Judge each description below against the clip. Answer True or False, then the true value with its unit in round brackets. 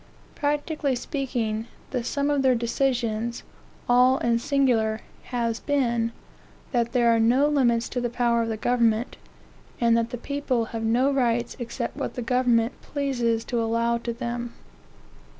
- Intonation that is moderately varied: False (2.2 semitones)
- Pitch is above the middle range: True (240 Hz)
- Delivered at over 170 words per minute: False (150 wpm)